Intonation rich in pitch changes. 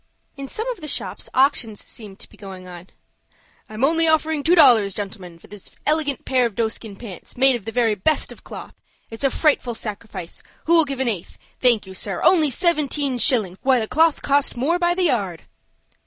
Yes: wide, 6.6 semitones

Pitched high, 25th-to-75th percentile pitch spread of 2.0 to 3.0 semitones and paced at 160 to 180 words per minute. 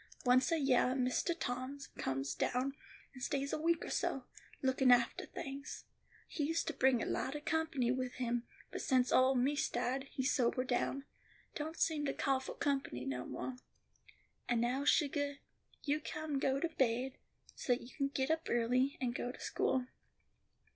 Yes: very high, 265 Hz; narrow, 2.4 semitones; average, 175 wpm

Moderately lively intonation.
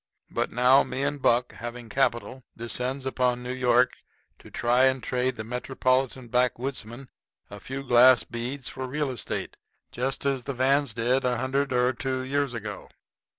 No: narrow, 1.6 semitones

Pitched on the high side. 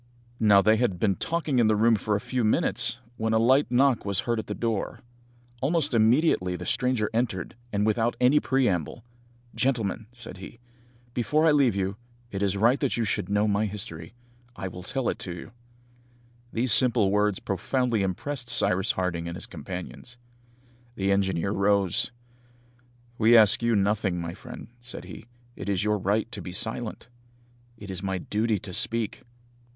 No: low, 110 Hz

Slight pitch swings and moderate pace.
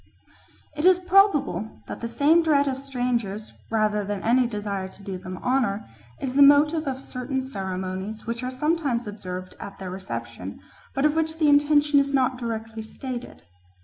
No: wide, 5.6 semitones; average, 170 wpm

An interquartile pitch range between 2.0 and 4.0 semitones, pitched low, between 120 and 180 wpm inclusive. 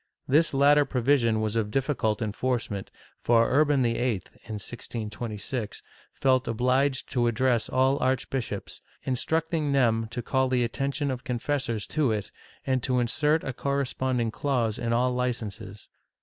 Yes: average, 3.0 semitones; low, 125 Hz; average, 140 wpm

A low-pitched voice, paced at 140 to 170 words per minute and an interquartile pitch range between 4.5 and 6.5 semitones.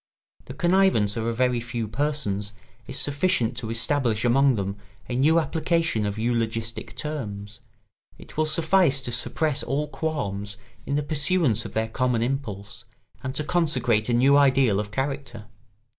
Yes: low, 125 Hz; average, 155 wpm; average, 4.8 semitones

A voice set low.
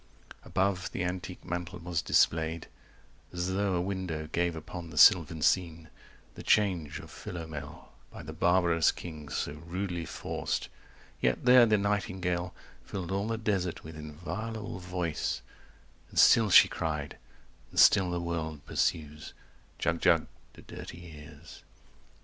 Yes: very low, 85 Hz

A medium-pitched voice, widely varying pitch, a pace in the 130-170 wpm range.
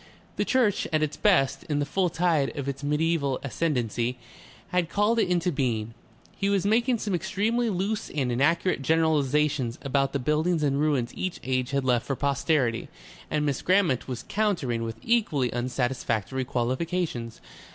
Yes: medium, 145 Hz; wide, 5.8 semitones; average, 160 wpm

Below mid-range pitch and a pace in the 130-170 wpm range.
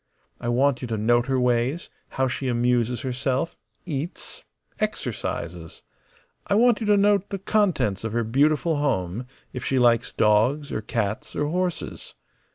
Yes: low, 125 Hz; average, 155 wpm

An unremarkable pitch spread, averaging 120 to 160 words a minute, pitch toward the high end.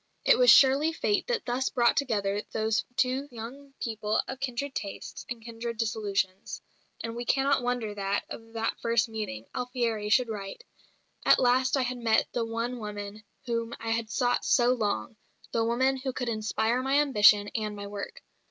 No: average, 3.0 semitones; average, 175 wpm; high, 230 Hz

